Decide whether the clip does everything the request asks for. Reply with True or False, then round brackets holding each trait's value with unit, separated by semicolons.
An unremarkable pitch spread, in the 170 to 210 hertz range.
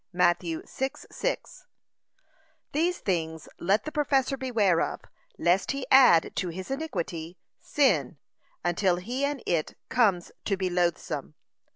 False (7.6 semitones; 190 Hz)